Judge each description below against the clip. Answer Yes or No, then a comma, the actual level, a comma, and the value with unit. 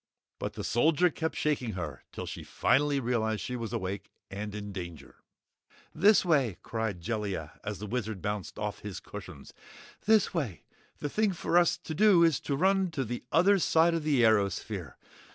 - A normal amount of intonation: No, wide, 8.0 semitones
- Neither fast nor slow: Yes, average, 175 wpm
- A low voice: Yes, low, 120 Hz